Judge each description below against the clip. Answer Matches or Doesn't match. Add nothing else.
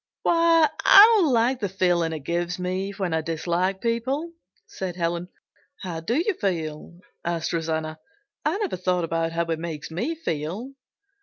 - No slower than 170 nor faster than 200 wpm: Doesn't match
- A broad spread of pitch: Matches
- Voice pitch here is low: Doesn't match